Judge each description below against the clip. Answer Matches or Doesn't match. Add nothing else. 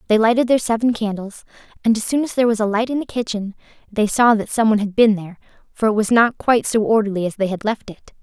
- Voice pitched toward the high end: Matches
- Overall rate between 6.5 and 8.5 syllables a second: Matches